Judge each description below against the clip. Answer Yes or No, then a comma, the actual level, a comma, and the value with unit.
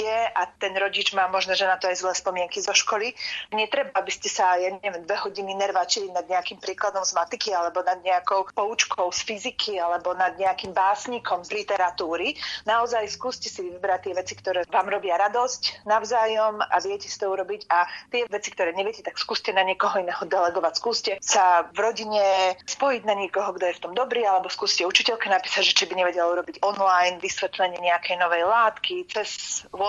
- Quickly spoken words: Yes, fast, 185 wpm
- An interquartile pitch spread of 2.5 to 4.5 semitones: Yes, average, 2.8 semitones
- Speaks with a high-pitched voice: Yes, high, 195 Hz